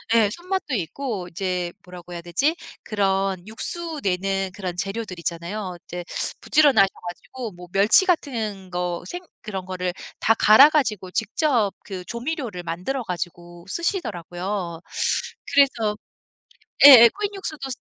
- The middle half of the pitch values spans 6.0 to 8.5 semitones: Yes, wide, 6.8 semitones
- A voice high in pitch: Yes, high, 200 Hz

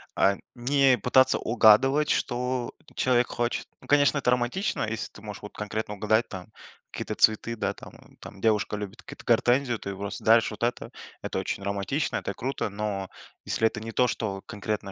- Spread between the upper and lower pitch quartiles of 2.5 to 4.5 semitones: Yes, average, 3.2 semitones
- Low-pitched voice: Yes, low, 115 Hz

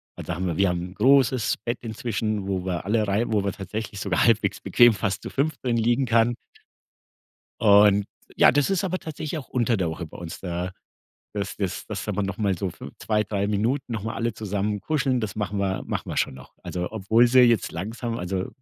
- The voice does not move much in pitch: No, average, 3.4 semitones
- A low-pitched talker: Yes, low, 105 Hz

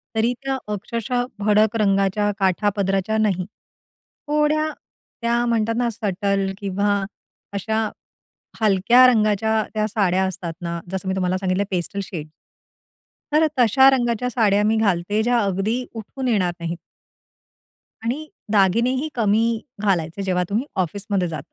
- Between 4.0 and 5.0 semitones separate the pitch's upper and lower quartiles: No, average, 3.4 semitones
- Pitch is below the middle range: No, high, 210 Hz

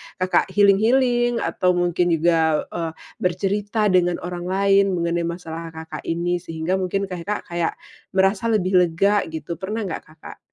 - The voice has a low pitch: No, medium, 180 Hz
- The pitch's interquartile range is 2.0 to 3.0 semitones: Yes, average, 2.7 semitones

